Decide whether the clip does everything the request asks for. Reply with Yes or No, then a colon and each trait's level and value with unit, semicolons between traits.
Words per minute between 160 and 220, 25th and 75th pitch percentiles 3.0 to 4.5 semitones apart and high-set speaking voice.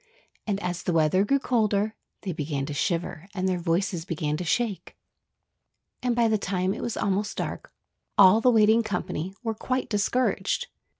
Yes: average, 170 wpm; average, 4.0 semitones; high, 195 Hz